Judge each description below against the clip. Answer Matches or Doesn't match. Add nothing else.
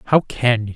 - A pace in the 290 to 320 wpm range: Doesn't match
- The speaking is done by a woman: Doesn't match